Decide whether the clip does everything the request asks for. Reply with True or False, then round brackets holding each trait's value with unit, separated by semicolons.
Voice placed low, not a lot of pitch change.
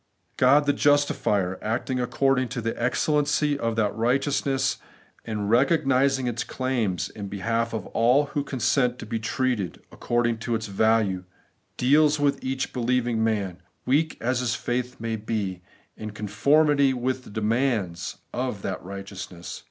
False (120 Hz; 3.8 semitones)